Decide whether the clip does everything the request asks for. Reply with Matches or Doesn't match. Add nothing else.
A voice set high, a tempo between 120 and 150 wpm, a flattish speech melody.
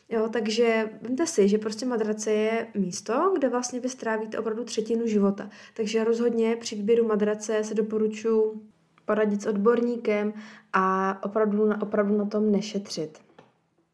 Matches